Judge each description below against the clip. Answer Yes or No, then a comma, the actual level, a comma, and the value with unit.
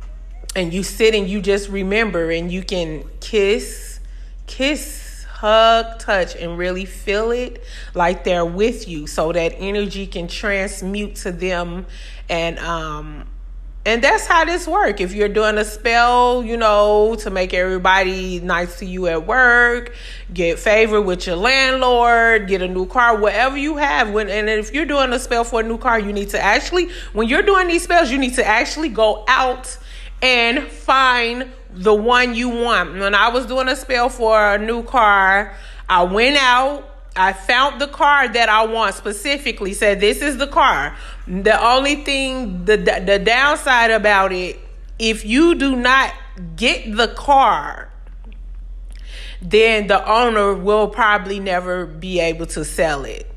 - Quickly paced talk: No, average, 165 wpm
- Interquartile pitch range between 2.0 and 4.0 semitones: No, average, 4.7 semitones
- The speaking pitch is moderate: No, high, 220 Hz